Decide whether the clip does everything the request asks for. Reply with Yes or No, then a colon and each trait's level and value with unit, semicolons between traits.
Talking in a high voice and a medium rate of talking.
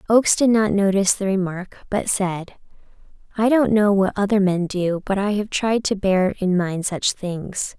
Yes: high, 195 Hz; average, 195 wpm